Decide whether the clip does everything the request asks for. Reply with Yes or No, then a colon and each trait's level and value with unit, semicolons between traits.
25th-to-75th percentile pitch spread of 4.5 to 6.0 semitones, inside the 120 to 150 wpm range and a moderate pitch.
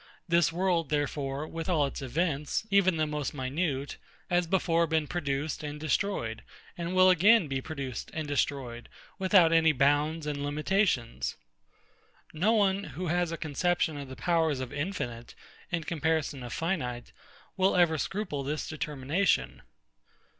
No: average, 3.9 semitones; average, 145 wpm; medium, 155 Hz